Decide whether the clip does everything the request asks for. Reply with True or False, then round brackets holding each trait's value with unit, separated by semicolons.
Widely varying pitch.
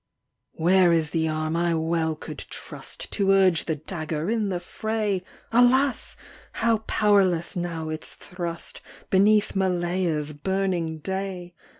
False (3.3 semitones)